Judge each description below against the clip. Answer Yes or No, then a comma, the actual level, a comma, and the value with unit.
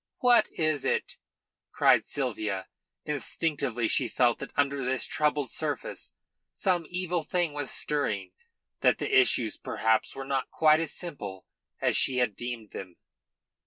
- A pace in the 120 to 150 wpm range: Yes, average, 140 wpm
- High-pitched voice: No, low, 135 Hz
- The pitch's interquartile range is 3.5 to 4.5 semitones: No, average, 4.9 semitones